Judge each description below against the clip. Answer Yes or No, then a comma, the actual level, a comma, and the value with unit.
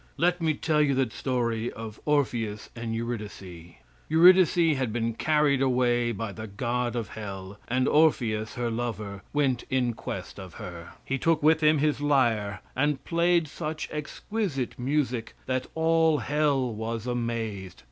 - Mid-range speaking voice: No, low, 125 Hz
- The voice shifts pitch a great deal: No, average, 5.0 semitones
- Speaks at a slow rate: No, average, 150 wpm